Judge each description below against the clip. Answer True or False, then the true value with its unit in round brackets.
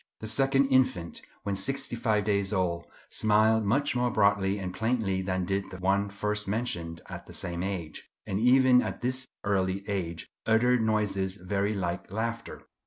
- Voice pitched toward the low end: True (100 Hz)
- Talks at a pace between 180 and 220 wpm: False (165 wpm)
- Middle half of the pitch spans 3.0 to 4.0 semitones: True (3.3 semitones)